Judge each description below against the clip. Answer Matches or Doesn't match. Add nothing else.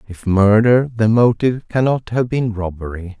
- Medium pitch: Doesn't match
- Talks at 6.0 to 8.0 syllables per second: Doesn't match